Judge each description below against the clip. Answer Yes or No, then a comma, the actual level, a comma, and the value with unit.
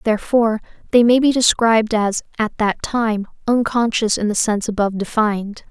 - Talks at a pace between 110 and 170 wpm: Yes, average, 160 wpm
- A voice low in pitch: No, high, 220 Hz